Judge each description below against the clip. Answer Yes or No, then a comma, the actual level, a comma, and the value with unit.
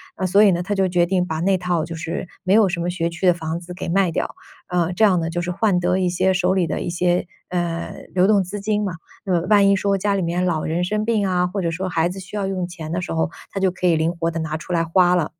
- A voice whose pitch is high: No, medium, 180 Hz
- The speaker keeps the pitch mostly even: Yes, narrow, 2.1 semitones